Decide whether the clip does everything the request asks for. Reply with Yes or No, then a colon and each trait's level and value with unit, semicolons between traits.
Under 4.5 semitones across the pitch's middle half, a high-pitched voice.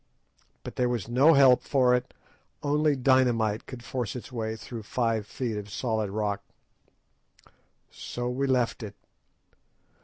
No: average, 2.9 semitones; low, 120 Hz